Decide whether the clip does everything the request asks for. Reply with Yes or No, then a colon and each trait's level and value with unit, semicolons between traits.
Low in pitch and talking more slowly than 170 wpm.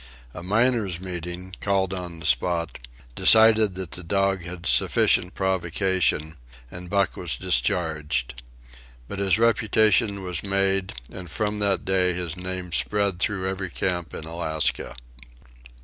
Yes: very low, 95 Hz; slow, 135 wpm